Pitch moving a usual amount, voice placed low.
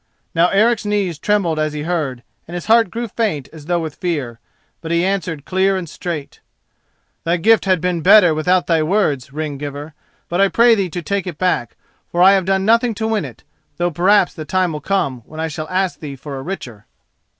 No: average, 4.2 semitones; medium, 175 Hz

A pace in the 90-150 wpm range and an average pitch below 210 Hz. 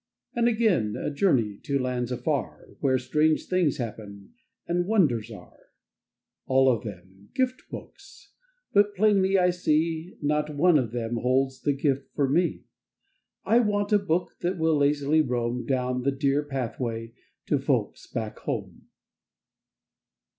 Yes: average, 145 wpm; medium, 140 Hz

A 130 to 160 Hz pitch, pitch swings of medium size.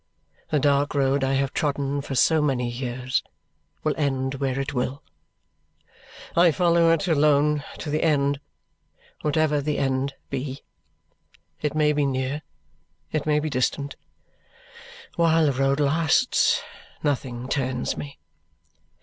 No: medium, 140 Hz; narrow, 2.1 semitones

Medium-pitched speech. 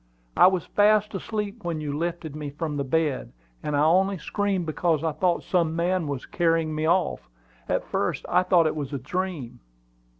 Yes: medium, 165 Hz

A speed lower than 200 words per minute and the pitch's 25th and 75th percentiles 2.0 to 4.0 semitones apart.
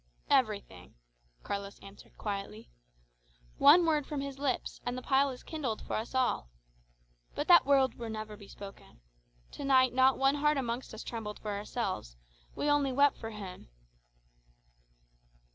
No: average, 150 wpm; average, 4.9 semitones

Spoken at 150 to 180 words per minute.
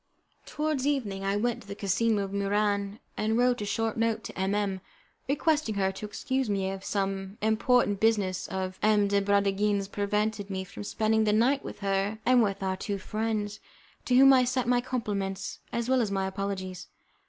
No: average, 190 wpm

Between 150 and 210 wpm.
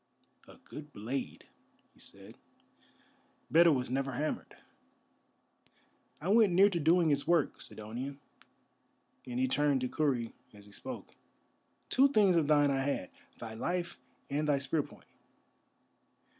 No: slow, 135 wpm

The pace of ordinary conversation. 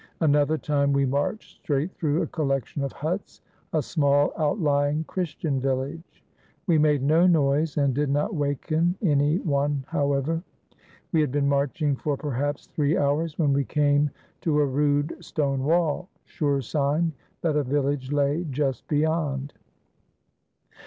Yes: average, 150 wpm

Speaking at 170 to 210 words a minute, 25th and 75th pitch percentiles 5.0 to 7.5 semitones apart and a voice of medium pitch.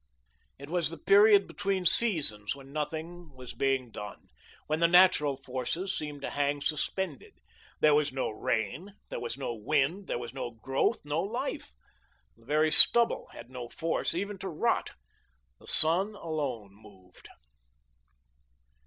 No: average, 145 wpm; wide, 5.6 semitones; medium, 150 Hz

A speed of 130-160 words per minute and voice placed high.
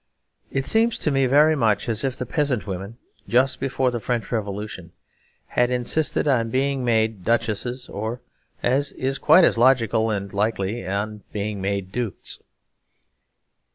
No: average, 150 wpm; low, 120 Hz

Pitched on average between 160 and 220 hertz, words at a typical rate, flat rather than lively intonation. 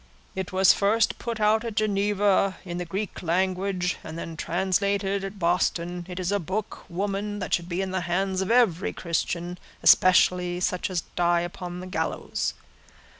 Yes: medium, 185 Hz; average, 170 wpm; narrow, 2.2 semitones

